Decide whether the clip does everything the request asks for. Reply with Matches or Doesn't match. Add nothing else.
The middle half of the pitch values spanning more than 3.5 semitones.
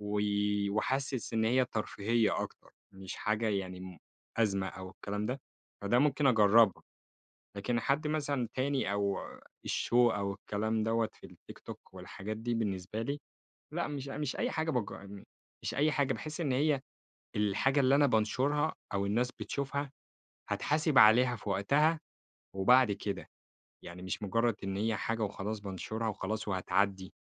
Matches